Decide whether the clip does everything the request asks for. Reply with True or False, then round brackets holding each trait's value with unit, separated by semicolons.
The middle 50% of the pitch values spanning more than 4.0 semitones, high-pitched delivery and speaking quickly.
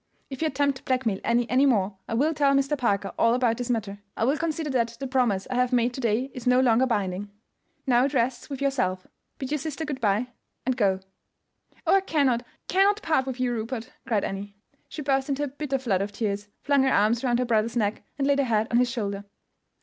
False (3.7 semitones; 250 Hz; 230 wpm)